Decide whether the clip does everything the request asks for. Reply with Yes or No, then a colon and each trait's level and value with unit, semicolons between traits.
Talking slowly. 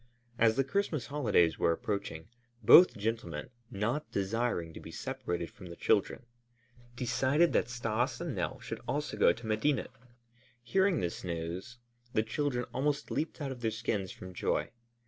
No: average, 155 wpm